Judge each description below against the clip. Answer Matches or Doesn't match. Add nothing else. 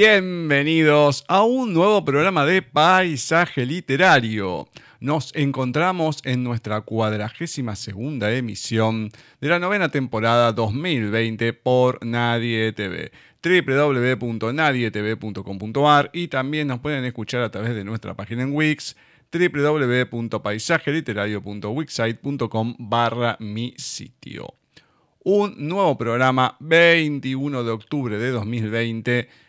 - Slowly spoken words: Matches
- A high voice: Doesn't match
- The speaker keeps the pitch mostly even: Doesn't match